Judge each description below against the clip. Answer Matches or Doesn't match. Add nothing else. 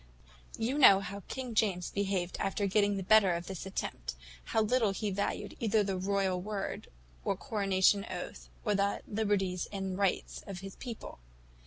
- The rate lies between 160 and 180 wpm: Matches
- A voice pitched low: Doesn't match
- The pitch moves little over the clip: Matches